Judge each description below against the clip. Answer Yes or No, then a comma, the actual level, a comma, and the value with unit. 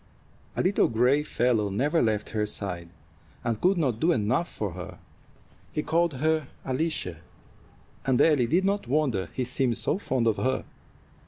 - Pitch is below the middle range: Yes, low, 130 Hz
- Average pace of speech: Yes, average, 160 wpm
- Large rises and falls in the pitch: Yes, wide, 6.3 semitones